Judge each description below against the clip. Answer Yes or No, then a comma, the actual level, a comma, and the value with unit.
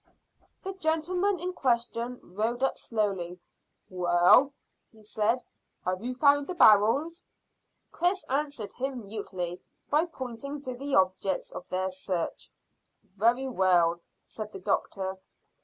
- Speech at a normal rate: No, slow, 125 wpm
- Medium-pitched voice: No, high, 230 Hz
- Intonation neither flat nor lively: No, wide, 7.0 semitones